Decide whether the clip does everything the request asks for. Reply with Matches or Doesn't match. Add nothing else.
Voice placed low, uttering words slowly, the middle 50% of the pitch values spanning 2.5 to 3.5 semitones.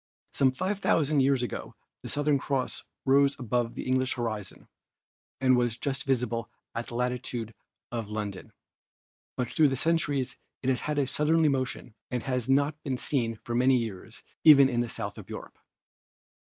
Doesn't match